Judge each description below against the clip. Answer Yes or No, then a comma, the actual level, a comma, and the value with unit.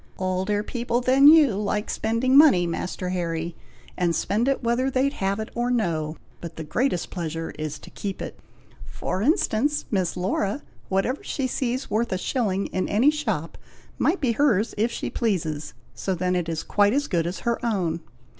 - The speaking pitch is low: No, high, 205 Hz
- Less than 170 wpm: No, average, 175 wpm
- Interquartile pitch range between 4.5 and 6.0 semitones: Yes, wide, 5.6 semitones